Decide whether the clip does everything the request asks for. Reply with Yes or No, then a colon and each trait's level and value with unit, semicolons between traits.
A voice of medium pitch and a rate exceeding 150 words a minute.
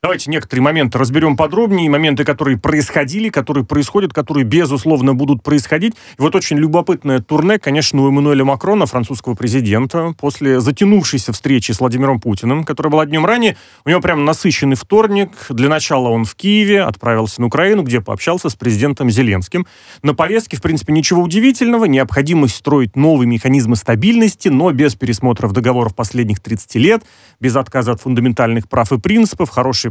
Yes: medium, 145 Hz; fast, 160 wpm